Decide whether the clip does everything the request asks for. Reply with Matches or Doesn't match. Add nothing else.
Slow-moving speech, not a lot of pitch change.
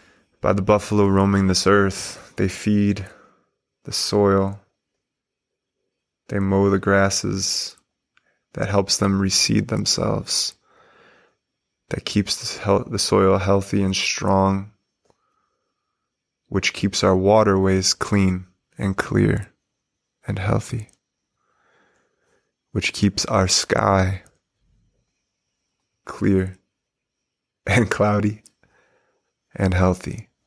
Matches